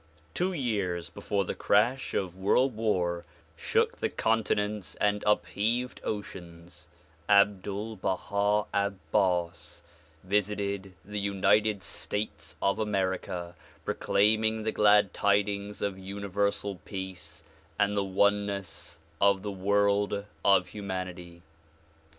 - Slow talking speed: Yes, slow, 105 wpm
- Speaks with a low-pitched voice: Yes, low, 100 Hz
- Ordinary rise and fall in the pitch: No, narrow, 1.6 semitones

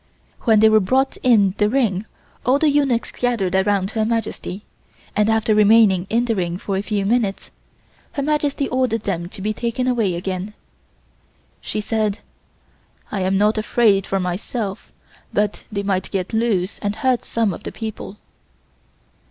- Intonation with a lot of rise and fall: No, average, 3.1 semitones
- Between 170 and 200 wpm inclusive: No, average, 160 wpm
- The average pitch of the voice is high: Yes, high, 215 Hz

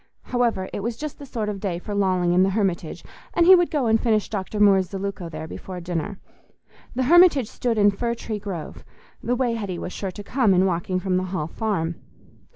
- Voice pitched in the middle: No, high, 200 Hz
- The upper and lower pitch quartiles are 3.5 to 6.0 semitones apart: Yes, average, 4.1 semitones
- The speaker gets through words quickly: Yes, fast, 210 wpm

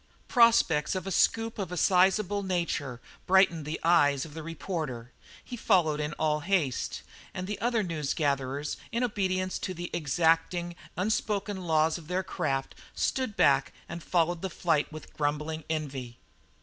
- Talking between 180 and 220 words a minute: No, average, 155 wpm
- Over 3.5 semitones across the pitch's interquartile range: Yes, average, 3.9 semitones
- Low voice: No, medium, 170 Hz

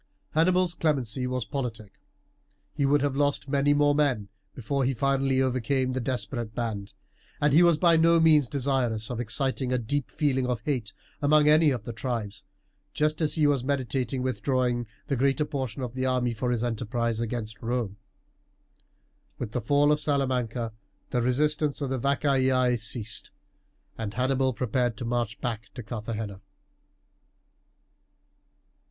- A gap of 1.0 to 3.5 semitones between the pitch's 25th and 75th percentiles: Yes, average, 3.2 semitones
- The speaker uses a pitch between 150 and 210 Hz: No, low, 130 Hz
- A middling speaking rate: Yes, average, 150 wpm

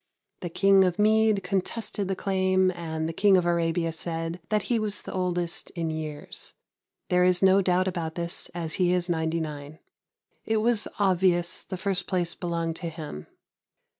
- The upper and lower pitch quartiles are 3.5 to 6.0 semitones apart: No, narrow, 2.6 semitones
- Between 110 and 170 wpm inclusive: Yes, average, 165 wpm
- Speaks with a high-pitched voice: No, medium, 180 Hz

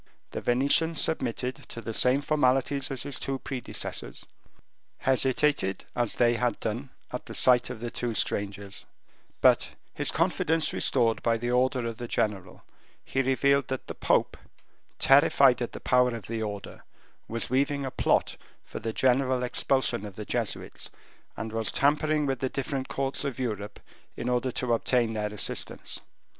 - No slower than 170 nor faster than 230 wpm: No, average, 160 wpm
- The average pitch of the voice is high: No, low, 125 Hz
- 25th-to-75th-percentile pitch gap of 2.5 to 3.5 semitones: Yes, average, 2.8 semitones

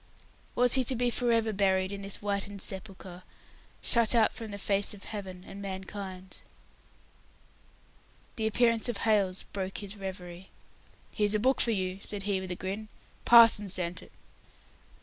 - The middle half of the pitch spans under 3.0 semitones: Yes, narrow, 2.6 semitones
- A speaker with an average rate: Yes, average, 160 wpm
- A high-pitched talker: Yes, high, 200 Hz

